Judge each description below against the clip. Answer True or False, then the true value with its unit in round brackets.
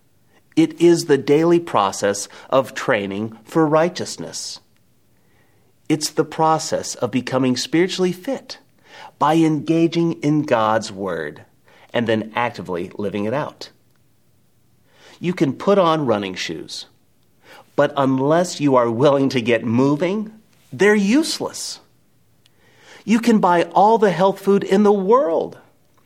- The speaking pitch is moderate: True (155 Hz)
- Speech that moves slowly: True (120 wpm)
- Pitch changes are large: True (6.5 semitones)